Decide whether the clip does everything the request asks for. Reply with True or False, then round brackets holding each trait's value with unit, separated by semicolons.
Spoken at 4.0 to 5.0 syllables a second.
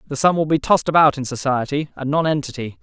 False (6.6 syllables/s)